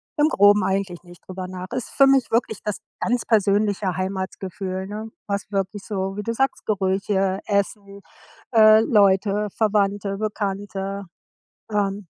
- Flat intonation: Yes, narrow, 1.8 semitones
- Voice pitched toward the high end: Yes, high, 200 Hz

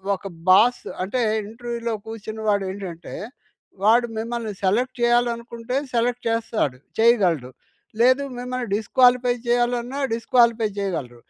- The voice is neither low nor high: No, high, 235 Hz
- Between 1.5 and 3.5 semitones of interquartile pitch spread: Yes, narrow, 2.6 semitones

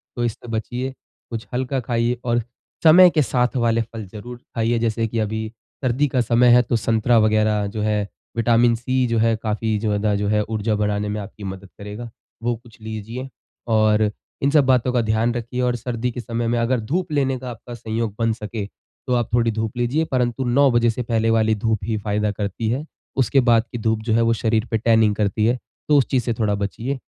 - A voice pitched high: No, low, 115 Hz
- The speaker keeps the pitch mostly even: Yes, narrow, 2.2 semitones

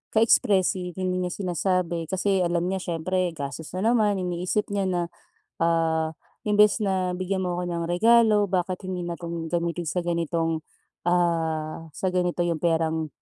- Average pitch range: No, narrow, 2.0 semitones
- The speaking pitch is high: No, medium, 175 Hz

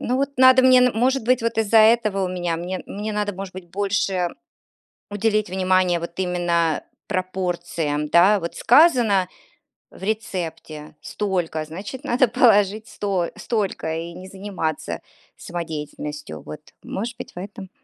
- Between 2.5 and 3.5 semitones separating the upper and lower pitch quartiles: No, average, 4.1 semitones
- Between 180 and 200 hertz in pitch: Yes, high, 190 Hz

